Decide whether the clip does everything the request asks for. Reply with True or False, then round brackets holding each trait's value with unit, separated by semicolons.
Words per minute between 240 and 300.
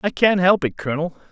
False (230 wpm)